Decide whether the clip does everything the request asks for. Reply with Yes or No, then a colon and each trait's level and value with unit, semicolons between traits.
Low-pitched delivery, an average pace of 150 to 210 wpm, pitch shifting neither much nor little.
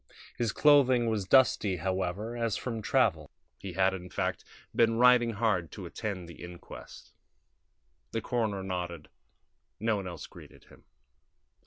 No: low, 105 Hz; average, 140 wpm; average, 4.1 semitones